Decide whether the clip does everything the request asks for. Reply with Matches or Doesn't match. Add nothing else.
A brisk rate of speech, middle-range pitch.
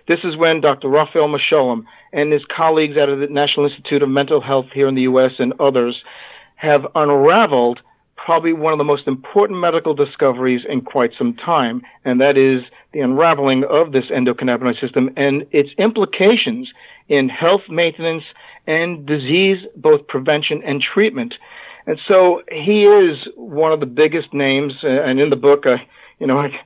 Doesn't match